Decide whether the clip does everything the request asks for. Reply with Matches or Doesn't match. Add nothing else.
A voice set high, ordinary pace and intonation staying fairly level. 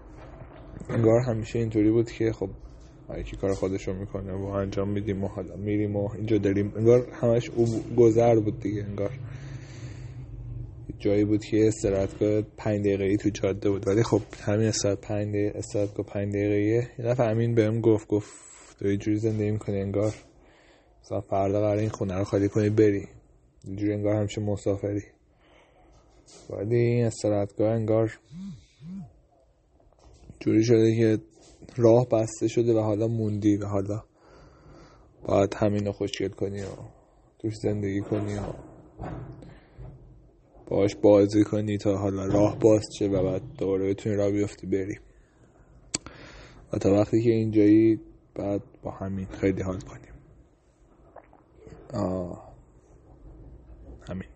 Doesn't match